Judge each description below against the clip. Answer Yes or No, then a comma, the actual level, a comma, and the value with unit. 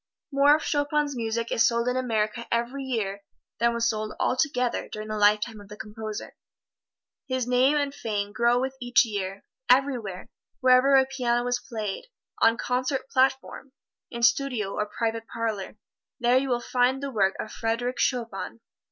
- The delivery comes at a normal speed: Yes, average, 160 wpm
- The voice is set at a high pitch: Yes, high, 235 Hz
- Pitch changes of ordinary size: Yes, average, 3.0 semitones